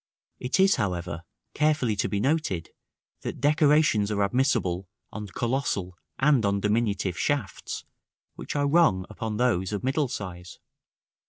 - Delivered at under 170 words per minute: Yes, average, 145 wpm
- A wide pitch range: Yes, wide, 6.6 semitones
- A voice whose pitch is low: Yes, low, 110 Hz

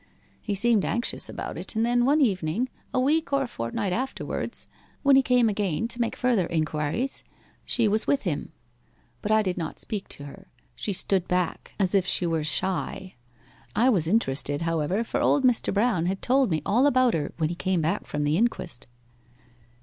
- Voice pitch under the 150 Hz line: No, high, 200 Hz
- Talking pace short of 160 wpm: No, average, 190 wpm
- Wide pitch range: Yes, wide, 6.3 semitones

